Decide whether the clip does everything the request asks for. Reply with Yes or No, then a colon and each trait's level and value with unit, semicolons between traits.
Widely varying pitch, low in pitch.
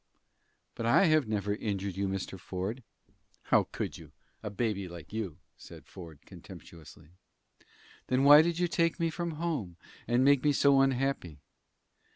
Yes: wide, 7.1 semitones; low, 115 Hz